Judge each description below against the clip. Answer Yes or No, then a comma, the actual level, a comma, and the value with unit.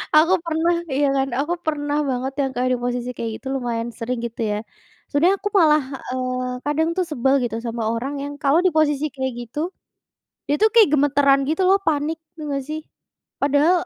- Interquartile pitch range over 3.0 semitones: Yes, average, 3.6 semitones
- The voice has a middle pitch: No, very high, 285 Hz